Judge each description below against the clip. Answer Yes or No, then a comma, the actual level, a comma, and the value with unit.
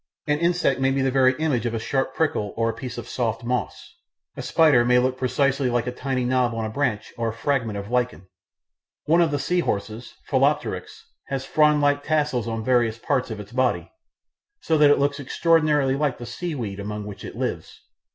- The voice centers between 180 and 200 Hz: No, low, 130 Hz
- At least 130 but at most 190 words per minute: No, fast, 205 wpm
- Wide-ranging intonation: No, average, 3.7 semitones